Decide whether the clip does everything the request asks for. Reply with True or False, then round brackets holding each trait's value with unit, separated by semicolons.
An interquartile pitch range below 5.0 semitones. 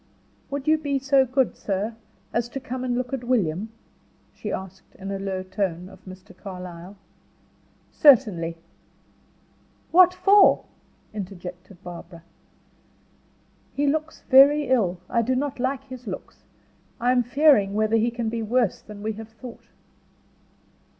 False (5.5 semitones)